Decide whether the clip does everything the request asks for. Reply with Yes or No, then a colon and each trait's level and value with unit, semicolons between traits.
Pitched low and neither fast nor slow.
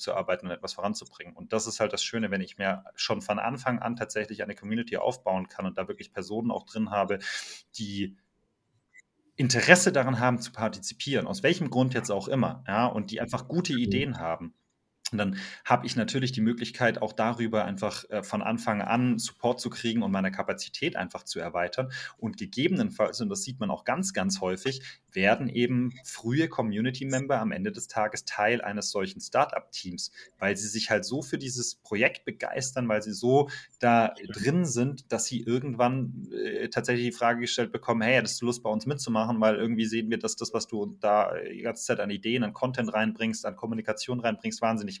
No: low, 115 Hz; fast, 195 wpm